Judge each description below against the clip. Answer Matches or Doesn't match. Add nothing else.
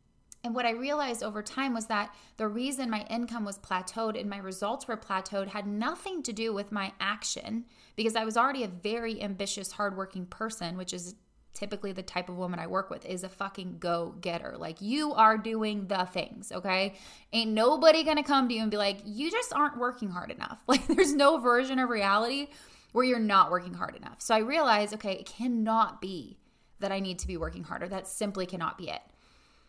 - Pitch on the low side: Doesn't match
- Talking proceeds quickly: Matches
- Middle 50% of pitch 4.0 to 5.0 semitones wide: Doesn't match